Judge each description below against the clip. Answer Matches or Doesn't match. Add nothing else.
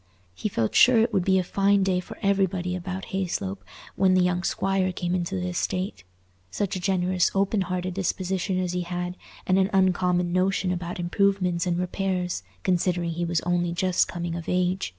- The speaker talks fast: Doesn't match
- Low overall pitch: Doesn't match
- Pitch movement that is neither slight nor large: Doesn't match